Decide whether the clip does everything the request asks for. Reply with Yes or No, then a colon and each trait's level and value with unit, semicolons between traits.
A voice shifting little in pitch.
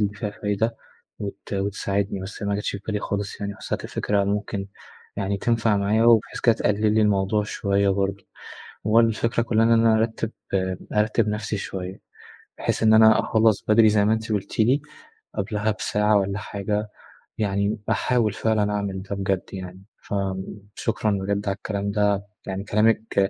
Yes: narrow, 1.7 semitones